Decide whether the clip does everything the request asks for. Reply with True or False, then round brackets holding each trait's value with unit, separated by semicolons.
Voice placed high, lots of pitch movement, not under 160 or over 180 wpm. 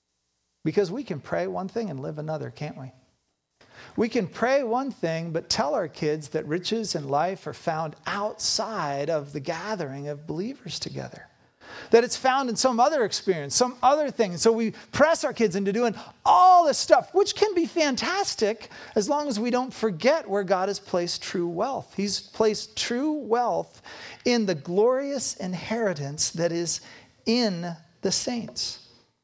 True (210 Hz; 6.7 semitones; 170 wpm)